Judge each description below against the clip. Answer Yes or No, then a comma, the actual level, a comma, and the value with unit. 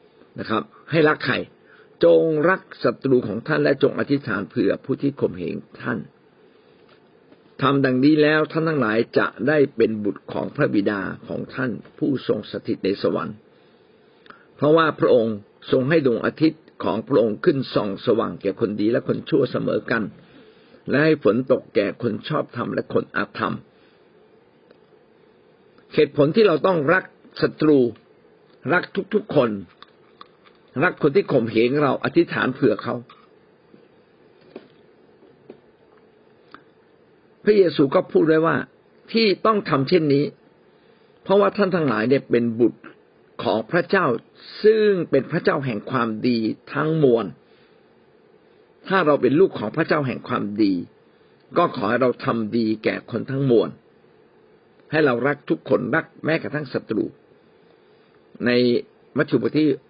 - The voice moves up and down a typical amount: No, wide, 9.0 semitones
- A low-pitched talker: No, medium, 155 Hz